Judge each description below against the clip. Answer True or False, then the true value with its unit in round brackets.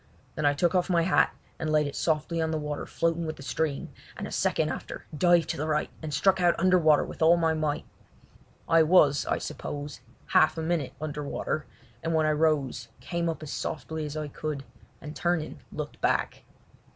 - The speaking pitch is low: False (155 Hz)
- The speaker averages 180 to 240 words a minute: True (205 wpm)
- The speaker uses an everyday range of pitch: False (1.9 semitones)